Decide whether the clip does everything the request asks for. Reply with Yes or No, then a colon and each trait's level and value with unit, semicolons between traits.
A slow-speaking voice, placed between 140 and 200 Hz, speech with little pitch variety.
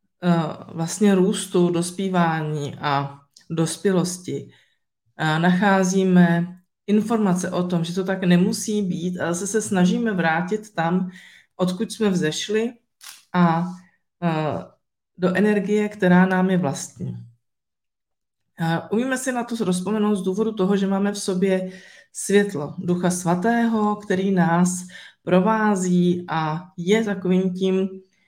No: slow, 110 wpm; medium, 185 Hz; average, 3.0 semitones